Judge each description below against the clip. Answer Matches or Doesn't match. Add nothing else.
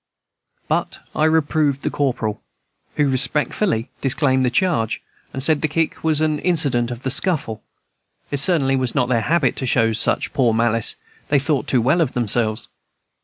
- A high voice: Doesn't match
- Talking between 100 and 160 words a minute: Doesn't match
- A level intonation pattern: Doesn't match